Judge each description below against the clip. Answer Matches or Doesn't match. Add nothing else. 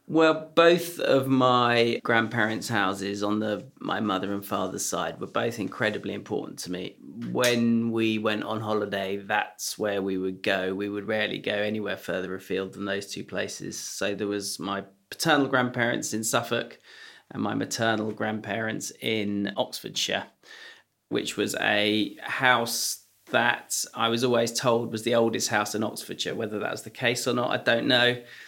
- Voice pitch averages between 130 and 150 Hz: Doesn't match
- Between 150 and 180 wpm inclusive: Matches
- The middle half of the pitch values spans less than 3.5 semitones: Matches